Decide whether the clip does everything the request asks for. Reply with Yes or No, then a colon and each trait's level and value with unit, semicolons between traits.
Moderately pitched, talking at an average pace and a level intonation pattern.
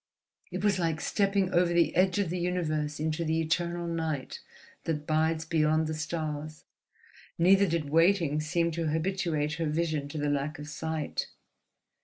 Yes: medium, 160 Hz; average, 160 wpm; narrow, 2.1 semitones